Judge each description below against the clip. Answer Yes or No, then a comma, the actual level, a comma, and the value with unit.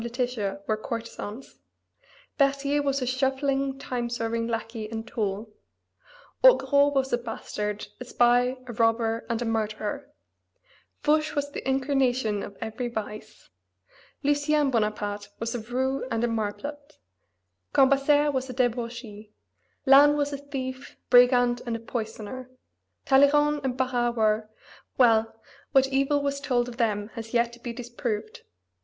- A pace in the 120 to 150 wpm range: Yes, slow, 135 wpm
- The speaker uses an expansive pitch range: No, average, 3.3 semitones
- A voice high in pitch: Yes, high, 245 Hz